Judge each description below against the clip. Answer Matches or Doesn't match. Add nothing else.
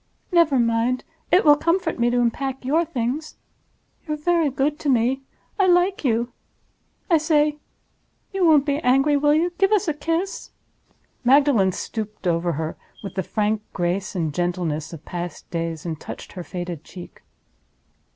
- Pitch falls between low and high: Doesn't match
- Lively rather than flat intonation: Matches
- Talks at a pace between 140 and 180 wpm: Matches